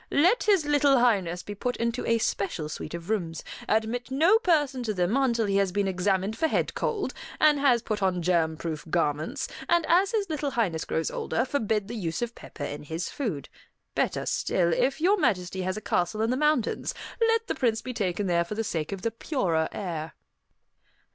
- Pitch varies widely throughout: Yes, wide, 7.5 semitones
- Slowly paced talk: No, average, 200 wpm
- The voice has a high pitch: Yes, high, 220 Hz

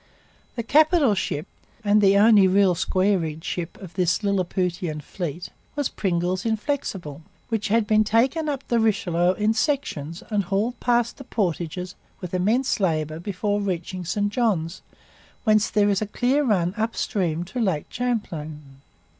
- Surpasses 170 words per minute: No, average, 150 wpm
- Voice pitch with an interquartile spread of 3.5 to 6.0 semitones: Yes, average, 4.2 semitones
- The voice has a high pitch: Yes, high, 200 Hz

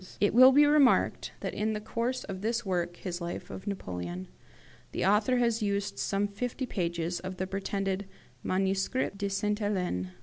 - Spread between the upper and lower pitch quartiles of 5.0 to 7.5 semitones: No, average, 3.1 semitones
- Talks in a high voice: Yes, high, 200 Hz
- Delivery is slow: No, average, 170 wpm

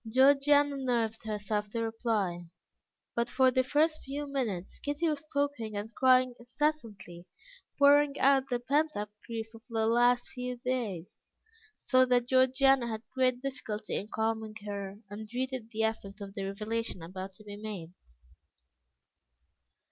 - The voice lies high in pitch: Yes, high, 235 Hz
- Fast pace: No, average, 145 wpm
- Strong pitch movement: No, average, 3.8 semitones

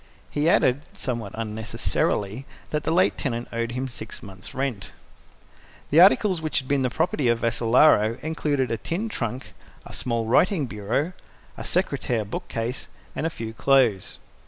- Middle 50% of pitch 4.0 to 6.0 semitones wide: Yes, average, 4.8 semitones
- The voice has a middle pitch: No, low, 125 Hz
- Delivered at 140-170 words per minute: Yes, average, 155 wpm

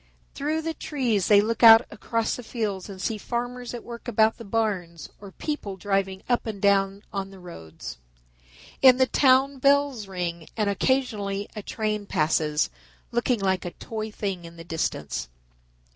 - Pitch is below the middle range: No, high, 210 Hz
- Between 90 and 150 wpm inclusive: No, average, 165 wpm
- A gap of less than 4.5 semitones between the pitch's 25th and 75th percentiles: Yes, average, 3.9 semitones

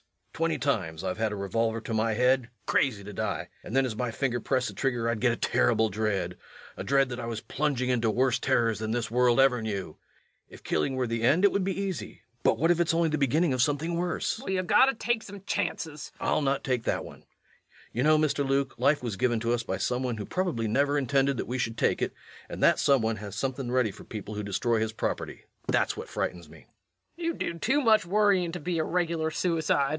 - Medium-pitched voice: No, low, 130 Hz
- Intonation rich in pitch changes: Yes, wide, 5.8 semitones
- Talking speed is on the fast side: Yes, fast, 240 wpm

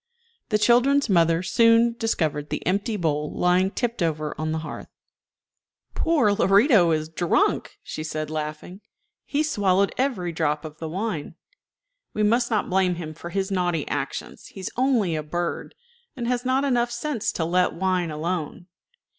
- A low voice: No, medium, 185 Hz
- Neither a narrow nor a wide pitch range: No, wide, 6.2 semitones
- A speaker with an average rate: Yes, average, 165 wpm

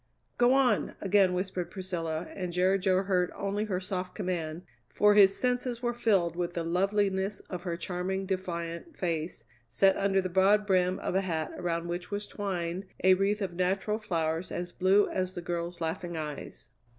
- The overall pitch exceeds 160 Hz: Yes, medium, 185 Hz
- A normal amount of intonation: No, narrow, 2.3 semitones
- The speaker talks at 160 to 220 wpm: Yes, average, 175 wpm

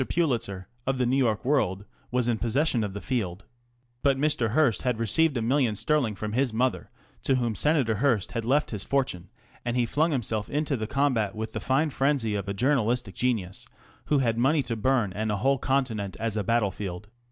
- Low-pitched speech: Yes, low, 120 Hz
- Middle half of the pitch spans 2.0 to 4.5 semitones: Yes, average, 4.1 semitones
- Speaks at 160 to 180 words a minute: No, average, 200 wpm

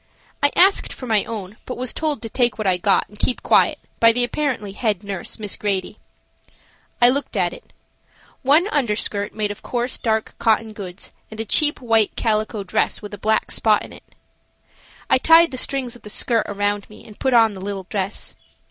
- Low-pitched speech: No, high, 220 Hz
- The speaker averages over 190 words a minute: Yes, average, 200 wpm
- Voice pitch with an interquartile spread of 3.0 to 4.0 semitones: Yes, average, 3.3 semitones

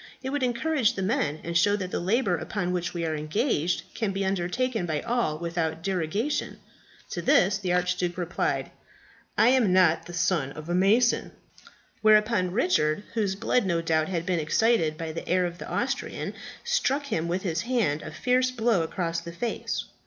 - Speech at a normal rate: Yes, average, 180 wpm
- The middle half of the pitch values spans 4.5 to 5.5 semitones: Yes, average, 5.1 semitones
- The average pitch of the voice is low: No, medium, 185 Hz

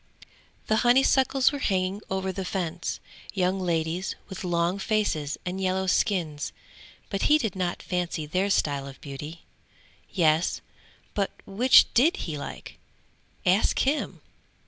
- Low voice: No, medium, 185 Hz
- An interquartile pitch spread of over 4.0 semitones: No, average, 3.3 semitones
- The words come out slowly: Yes, slow, 130 wpm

